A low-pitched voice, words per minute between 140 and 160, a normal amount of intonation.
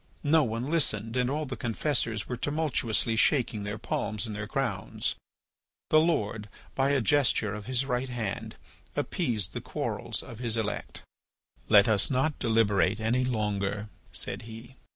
Yes: low, 115 Hz; average, 150 wpm; average, 3.7 semitones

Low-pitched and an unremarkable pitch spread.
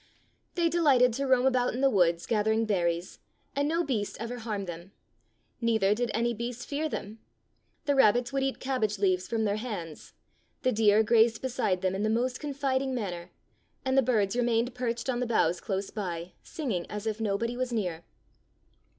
No: high, 230 Hz; average, 4.1 semitones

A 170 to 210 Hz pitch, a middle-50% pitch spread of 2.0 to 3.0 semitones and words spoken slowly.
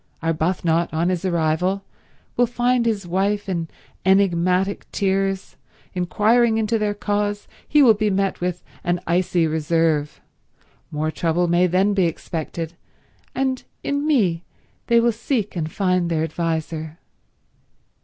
No: medium, 185 Hz; average, 3.8 semitones; slow, 130 wpm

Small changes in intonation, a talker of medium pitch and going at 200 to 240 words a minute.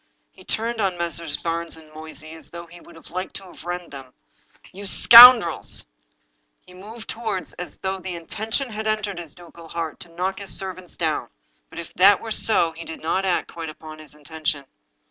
No: average, 3.2 semitones; medium, 175 Hz; fast, 205 wpm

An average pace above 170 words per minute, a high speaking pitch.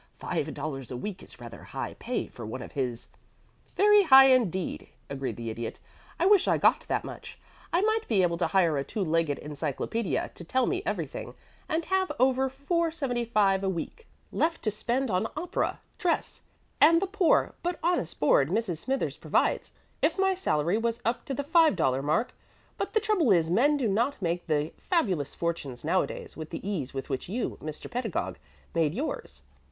Yes: average, 185 wpm; high, 210 Hz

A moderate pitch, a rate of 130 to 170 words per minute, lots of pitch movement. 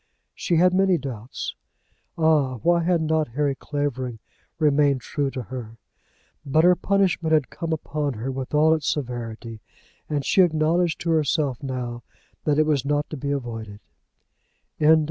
No: medium, 145 Hz; average, 150 wpm; average, 3.7 semitones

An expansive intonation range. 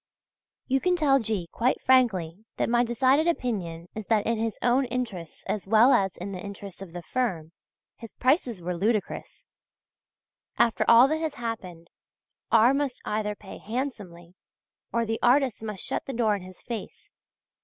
No: average, 4.6 semitones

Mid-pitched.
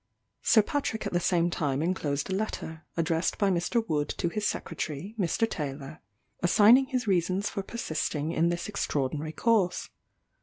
Yes: medium, 175 Hz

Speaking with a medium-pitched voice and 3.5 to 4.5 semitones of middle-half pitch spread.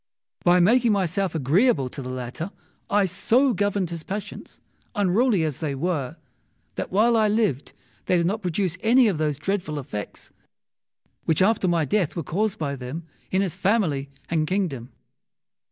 No: medium, 180 Hz; average, 5.2 semitones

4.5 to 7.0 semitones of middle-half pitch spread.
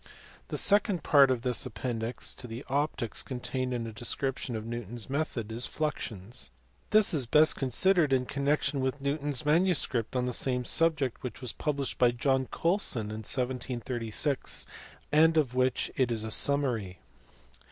No: average, 3.4 semitones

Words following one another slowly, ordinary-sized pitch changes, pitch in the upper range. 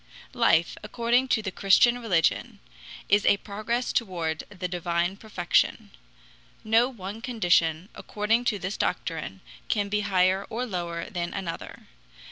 Yes: slow, 130 wpm; average, 4.3 semitones; high, 200 Hz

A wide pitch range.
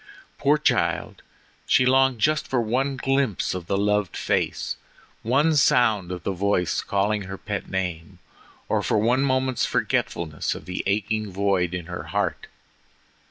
Yes: wide, 5.8 semitones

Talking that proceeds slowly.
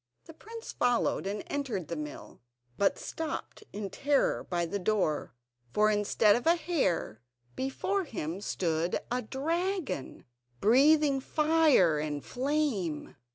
Yes: slow, 125 wpm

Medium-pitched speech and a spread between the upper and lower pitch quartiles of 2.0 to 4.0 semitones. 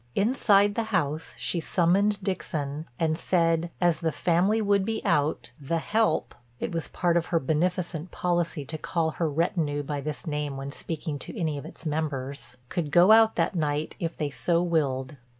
Yes: medium, 165 Hz; average, 3.4 semitones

